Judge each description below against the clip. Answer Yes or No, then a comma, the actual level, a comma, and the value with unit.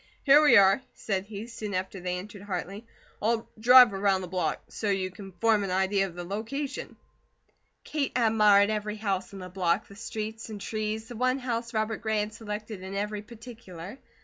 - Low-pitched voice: No, high, 210 Hz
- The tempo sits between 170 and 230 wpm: Yes, average, 190 wpm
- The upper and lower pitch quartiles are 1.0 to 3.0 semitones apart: Yes, narrow, 2.6 semitones